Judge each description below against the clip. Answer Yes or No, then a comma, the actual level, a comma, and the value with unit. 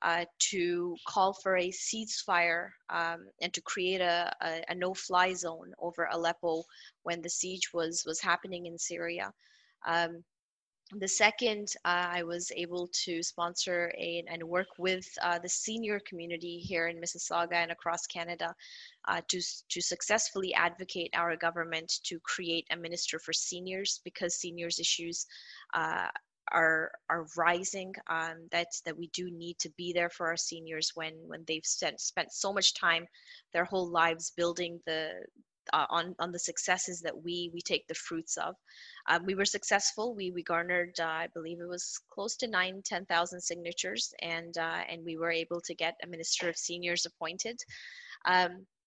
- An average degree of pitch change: No, narrow, 1.4 semitones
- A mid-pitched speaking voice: Yes, medium, 175 Hz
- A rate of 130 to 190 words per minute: Yes, average, 170 wpm